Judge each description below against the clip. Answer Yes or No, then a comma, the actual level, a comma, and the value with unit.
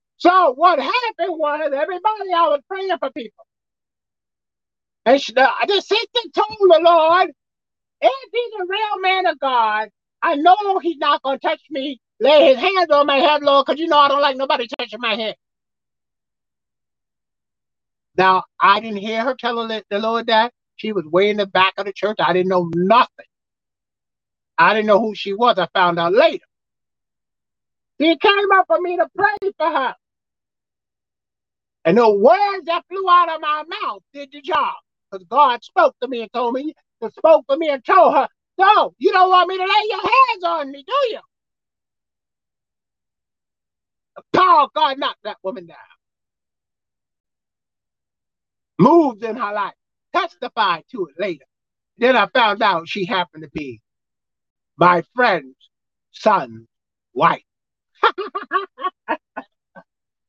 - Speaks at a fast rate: No, average, 155 wpm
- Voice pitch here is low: No, very high, 290 Hz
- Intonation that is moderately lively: No, wide, 8.6 semitones